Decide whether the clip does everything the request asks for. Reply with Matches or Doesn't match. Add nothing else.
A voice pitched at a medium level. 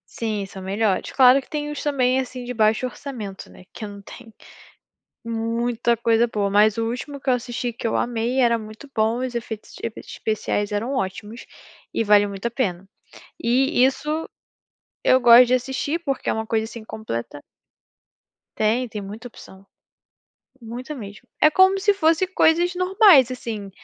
Doesn't match